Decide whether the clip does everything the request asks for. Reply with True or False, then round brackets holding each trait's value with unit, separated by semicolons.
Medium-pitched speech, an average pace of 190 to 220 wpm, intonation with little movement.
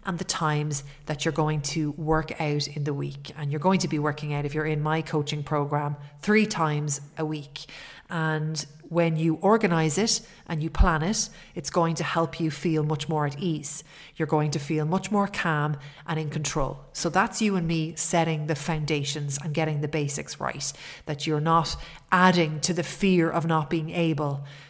True (155 Hz; 200 wpm; 1.9 semitones)